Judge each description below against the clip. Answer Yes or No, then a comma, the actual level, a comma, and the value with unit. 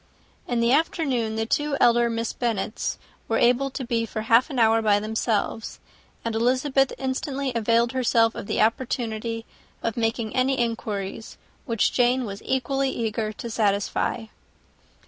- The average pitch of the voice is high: Yes, high, 235 Hz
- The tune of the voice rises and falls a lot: No, narrow, 2.5 semitones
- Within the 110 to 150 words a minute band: Yes, average, 145 wpm